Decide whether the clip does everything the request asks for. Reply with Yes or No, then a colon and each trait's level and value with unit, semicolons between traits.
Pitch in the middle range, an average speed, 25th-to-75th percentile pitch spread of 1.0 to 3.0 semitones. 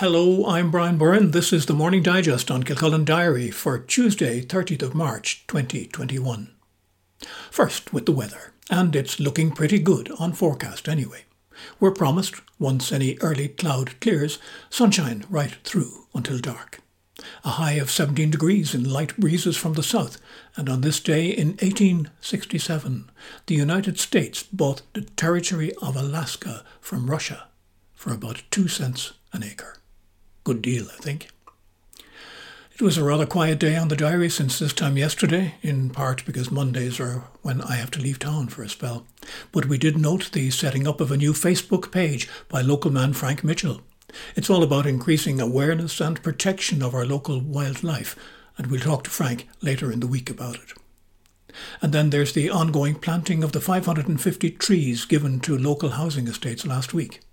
No: medium, 150 Hz; average, 170 wpm; average, 4.4 semitones